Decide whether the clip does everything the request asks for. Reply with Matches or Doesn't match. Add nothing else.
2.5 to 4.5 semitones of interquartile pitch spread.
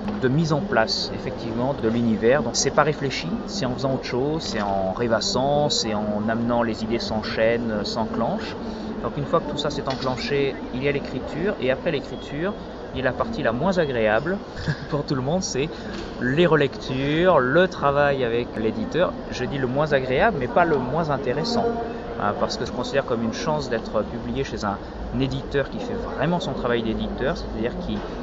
Doesn't match